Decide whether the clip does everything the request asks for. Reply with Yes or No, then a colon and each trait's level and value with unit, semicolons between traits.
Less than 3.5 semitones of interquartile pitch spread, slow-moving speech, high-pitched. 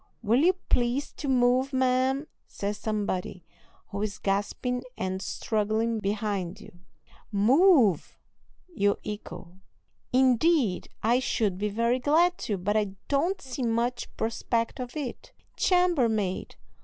No: average, 4.3 semitones; slow, 120 wpm; high, 230 Hz